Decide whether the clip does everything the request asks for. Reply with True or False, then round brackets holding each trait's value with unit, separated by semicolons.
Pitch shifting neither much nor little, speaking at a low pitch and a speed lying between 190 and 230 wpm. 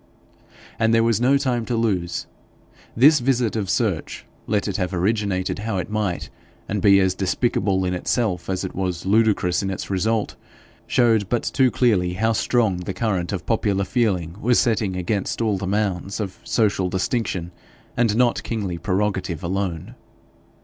False (3.6 semitones; 100 Hz; 165 wpm)